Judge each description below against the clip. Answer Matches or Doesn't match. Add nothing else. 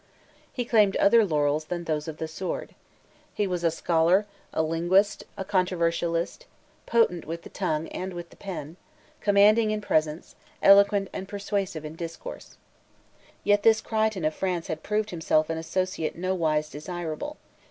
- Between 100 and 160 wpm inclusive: Matches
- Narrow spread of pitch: Doesn't match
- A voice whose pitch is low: Doesn't match